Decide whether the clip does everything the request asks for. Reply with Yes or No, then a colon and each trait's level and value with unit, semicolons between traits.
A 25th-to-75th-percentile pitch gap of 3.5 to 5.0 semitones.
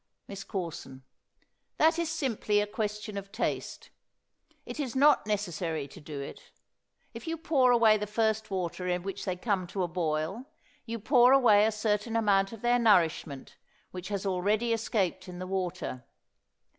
Yes: average, 4.1 semitones